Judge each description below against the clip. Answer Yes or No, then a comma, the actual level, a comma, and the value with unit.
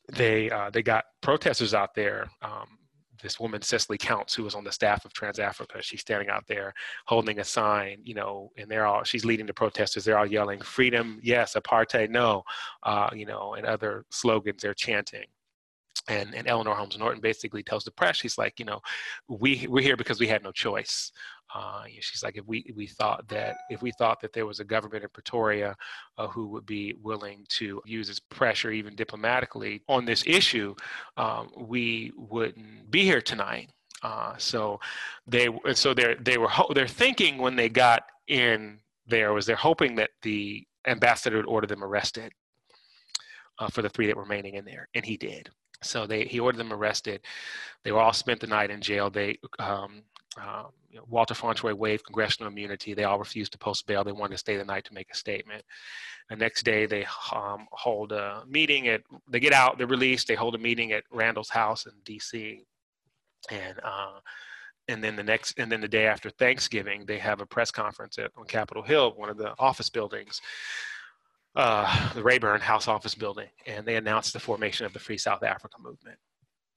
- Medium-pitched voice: No, low, 110 Hz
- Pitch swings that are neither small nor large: No, narrow, 1.9 semitones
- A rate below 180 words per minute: No, average, 200 wpm